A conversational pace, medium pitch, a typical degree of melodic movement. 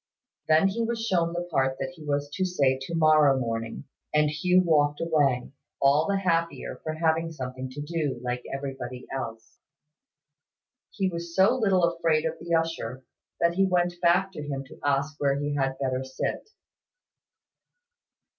Yes: average, 165 wpm; medium, 155 Hz; average, 4.0 semitones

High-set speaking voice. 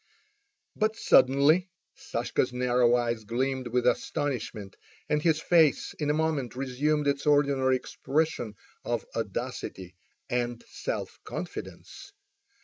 No: low, 135 Hz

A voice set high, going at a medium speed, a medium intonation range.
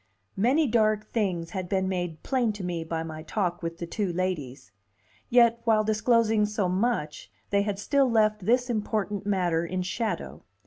Yes: high, 205 Hz; average, 170 wpm; average, 4.0 semitones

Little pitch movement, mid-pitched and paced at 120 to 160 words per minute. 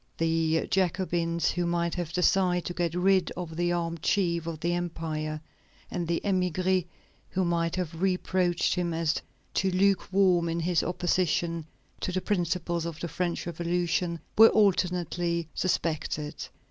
Yes: narrow, 1.5 semitones; medium, 175 Hz; average, 145 wpm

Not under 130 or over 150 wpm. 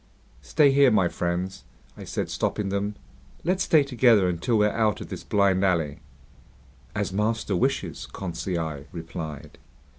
Yes: average, 140 wpm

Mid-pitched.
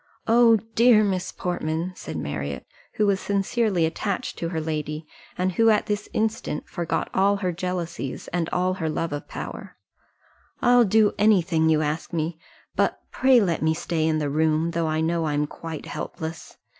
Yes: medium, 170 Hz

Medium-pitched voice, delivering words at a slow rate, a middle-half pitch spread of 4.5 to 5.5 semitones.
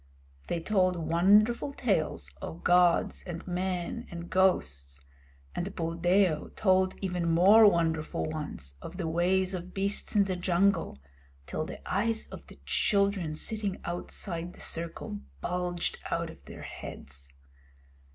No: medium, 180 Hz; slow, 130 wpm; average, 2.8 semitones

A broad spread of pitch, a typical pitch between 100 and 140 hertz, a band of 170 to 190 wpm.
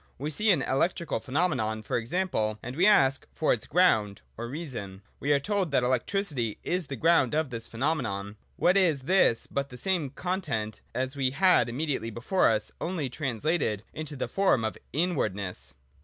Yes: wide, 6.8 semitones; low, 135 Hz; average, 175 wpm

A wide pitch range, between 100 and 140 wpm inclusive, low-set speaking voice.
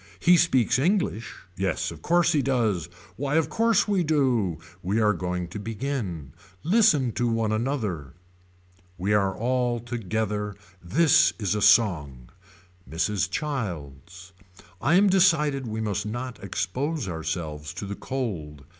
Yes: wide, 7.2 semitones; slow, 135 wpm; low, 110 Hz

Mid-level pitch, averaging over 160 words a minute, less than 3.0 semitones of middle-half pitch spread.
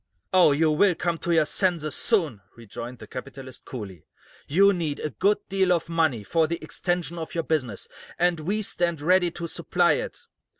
No: medium, 165 Hz; average, 180 wpm; average, 3.7 semitones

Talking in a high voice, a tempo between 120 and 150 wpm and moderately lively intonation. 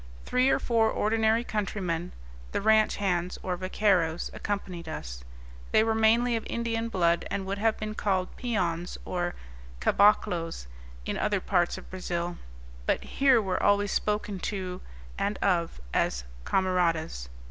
Yes: high, 195 Hz; average, 140 wpm; average, 3.8 semitones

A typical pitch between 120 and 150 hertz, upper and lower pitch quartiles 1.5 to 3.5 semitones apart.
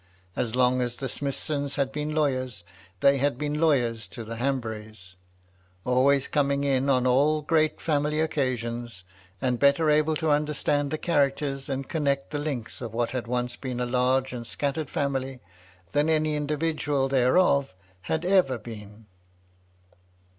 Yes: low, 135 Hz; average, 3.1 semitones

